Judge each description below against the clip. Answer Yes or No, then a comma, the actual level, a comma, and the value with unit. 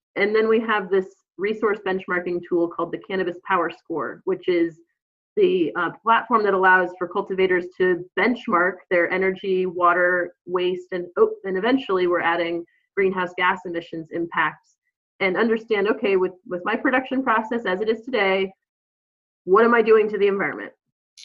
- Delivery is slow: No, average, 160 wpm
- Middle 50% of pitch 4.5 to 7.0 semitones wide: No, average, 3.8 semitones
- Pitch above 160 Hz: Yes, high, 190 Hz